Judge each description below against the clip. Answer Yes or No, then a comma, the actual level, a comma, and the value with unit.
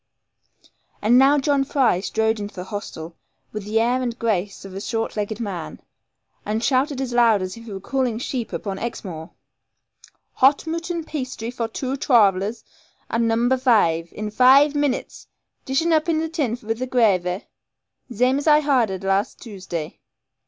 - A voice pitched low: No, high, 230 Hz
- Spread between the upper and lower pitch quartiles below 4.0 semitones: No, average, 4.7 semitones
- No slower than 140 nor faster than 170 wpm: Yes, average, 165 wpm